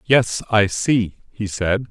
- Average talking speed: Yes, average, 155 wpm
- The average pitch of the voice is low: Yes, low, 110 Hz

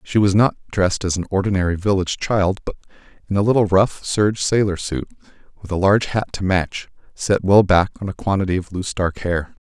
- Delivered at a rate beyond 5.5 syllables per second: Yes, 5.9 syllables/s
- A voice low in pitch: Yes, very low, 95 Hz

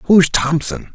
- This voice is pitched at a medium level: Yes, medium, 150 Hz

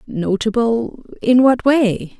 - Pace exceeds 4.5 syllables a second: No, 3.2 syllables/s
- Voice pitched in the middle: No, high, 235 Hz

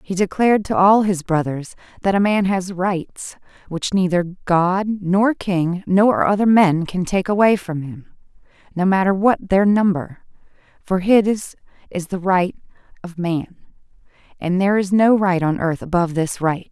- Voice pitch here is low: No, medium, 185 Hz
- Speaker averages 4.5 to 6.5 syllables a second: No, 4.3 syllables/s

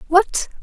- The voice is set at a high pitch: Yes, very high, 380 Hz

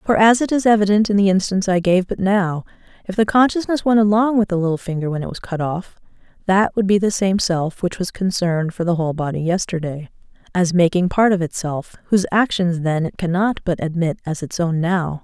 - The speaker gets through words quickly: Yes, fast, 220 wpm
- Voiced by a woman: Yes, female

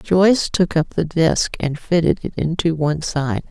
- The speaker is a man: No, female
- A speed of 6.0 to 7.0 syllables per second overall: No, 4.5 syllables/s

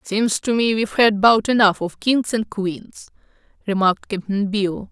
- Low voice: No, high, 210 Hz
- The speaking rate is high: No, average, 170 wpm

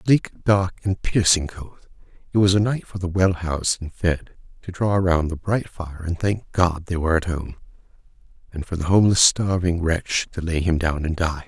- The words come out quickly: Yes, fast, 210 wpm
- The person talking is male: Yes, male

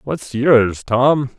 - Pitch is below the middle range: Yes, low, 125 Hz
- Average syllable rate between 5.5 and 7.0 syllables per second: No, 2.4 syllables/s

